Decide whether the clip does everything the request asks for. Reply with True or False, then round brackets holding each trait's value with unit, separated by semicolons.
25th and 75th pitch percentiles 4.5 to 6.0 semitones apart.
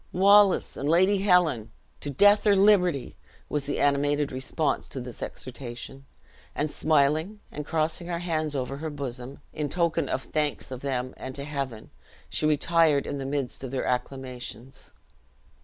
False (3.8 semitones)